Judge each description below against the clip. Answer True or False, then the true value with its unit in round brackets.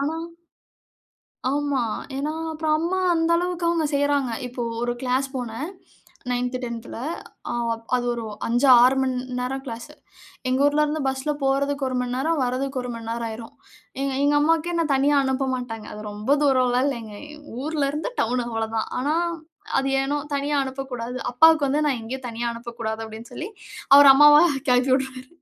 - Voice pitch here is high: True (265 Hz)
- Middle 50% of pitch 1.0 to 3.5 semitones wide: True (3.1 semitones)